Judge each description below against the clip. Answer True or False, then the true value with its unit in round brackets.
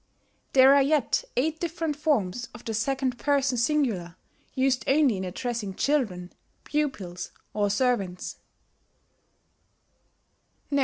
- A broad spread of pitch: True (5.9 semitones)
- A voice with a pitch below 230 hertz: False (250 Hz)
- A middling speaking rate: False (105 wpm)